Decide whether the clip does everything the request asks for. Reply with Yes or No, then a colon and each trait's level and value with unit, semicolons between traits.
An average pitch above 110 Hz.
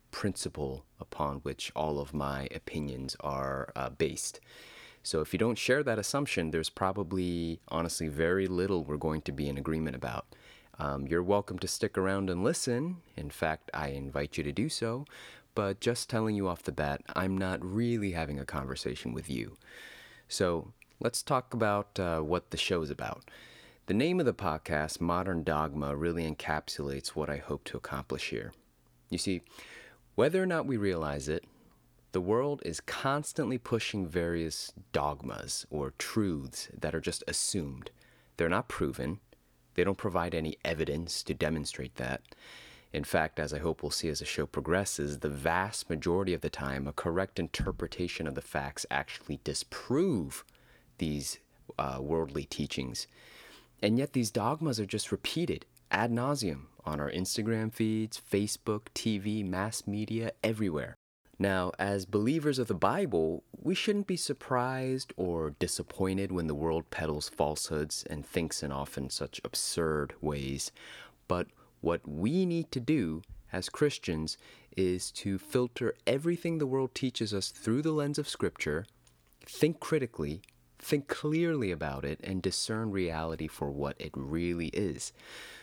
No: very low, 90 Hz